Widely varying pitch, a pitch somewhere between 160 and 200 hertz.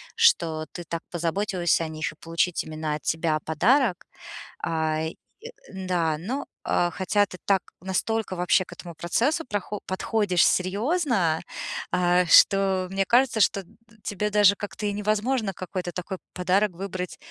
No: average, 3.4 semitones; medium, 185 Hz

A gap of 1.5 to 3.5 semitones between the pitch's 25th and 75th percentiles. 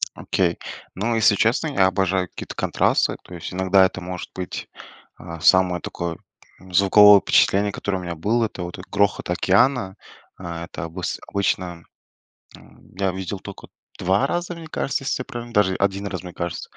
Yes: narrow, 2.5 semitones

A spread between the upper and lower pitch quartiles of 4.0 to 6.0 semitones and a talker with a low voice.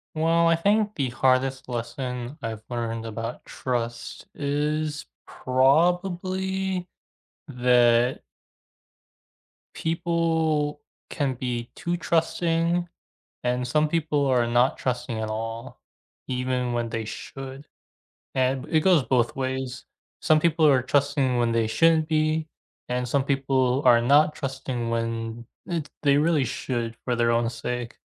Yes: average, 4.4 semitones; low, 130 Hz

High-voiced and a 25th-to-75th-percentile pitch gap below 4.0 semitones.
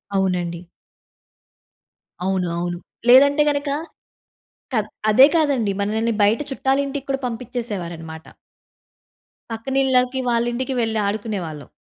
No: high, 225 Hz; wide, 5.5 semitones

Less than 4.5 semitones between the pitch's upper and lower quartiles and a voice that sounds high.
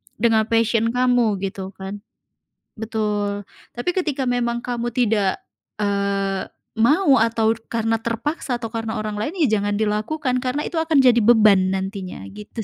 Yes: average, 3.1 semitones; high, 225 Hz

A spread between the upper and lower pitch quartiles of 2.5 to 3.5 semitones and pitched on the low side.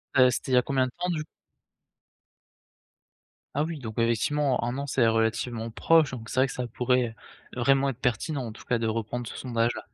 Yes: average, 2.9 semitones; low, 125 Hz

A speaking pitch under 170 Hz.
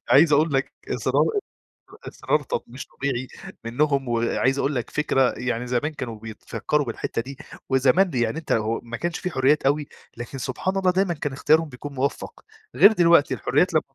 Yes: medium, 140 Hz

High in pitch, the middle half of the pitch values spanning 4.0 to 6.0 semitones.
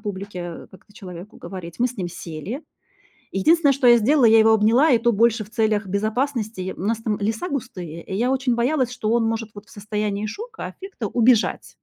No: high, 220 Hz; average, 3.3 semitones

